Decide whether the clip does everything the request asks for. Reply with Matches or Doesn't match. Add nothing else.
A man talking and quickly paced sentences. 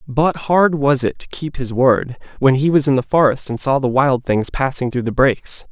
Matches